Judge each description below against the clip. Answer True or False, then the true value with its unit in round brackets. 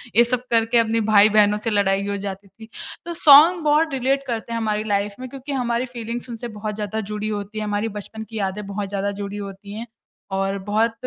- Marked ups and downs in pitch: False (2.7 semitones)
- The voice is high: True (215 Hz)